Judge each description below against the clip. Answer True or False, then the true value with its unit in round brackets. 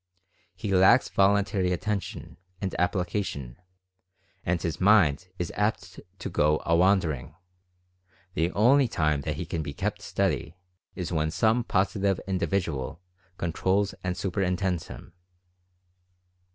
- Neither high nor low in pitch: False (90 Hz)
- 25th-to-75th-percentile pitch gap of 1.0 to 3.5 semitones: True (2.9 semitones)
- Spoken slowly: True (125 wpm)